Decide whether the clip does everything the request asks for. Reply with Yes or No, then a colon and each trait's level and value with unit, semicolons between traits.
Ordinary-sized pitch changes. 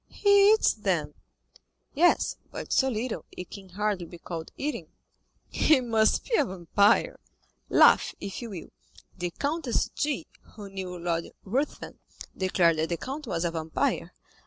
No: wide, 7.5 semitones